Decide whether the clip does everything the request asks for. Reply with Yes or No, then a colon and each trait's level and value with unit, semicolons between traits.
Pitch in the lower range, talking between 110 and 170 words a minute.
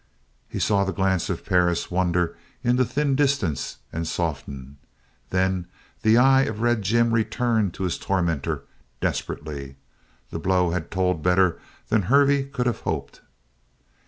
Yes: very low, 95 Hz; average, 140 wpm